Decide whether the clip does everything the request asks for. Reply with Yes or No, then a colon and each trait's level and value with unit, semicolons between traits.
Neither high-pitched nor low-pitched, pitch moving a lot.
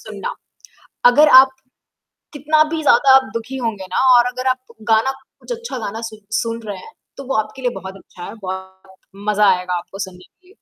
No: high, 225 Hz; wide, 5.7 semitones